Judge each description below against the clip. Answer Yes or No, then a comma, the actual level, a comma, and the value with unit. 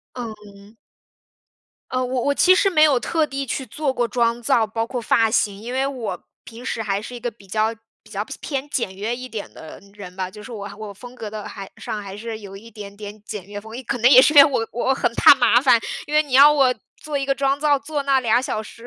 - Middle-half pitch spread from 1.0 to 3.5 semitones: No, average, 4.3 semitones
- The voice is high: Yes, high, 235 Hz